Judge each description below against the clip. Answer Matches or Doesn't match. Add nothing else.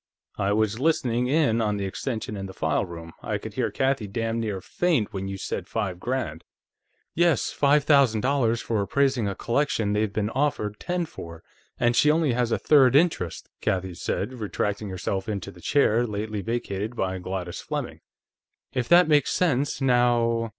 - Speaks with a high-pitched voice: Doesn't match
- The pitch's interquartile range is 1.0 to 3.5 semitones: Doesn't match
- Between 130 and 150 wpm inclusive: Doesn't match